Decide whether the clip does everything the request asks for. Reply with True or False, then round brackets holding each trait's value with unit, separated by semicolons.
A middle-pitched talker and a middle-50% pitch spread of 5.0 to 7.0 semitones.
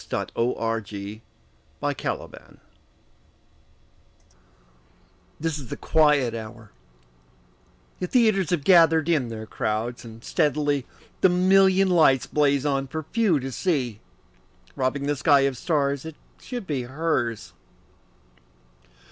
True (145 Hz; 5.3 semitones)